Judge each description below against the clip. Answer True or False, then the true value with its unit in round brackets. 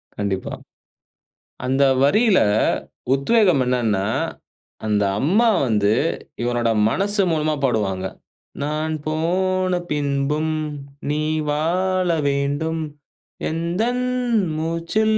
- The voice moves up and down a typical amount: False (5.8 semitones)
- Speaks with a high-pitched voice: False (155 Hz)